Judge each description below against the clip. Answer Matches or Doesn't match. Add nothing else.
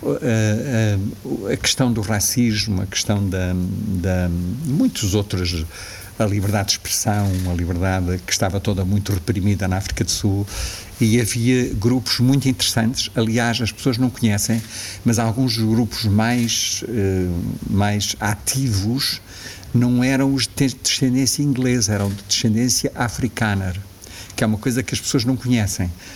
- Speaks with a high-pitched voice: Doesn't match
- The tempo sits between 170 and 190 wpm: Doesn't match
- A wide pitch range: Doesn't match